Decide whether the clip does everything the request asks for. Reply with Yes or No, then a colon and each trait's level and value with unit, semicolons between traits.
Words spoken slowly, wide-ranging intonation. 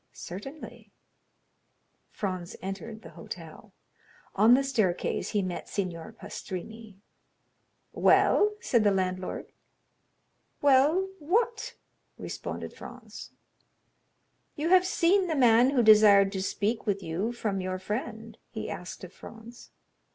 Yes: slow, 110 wpm; wide, 5.9 semitones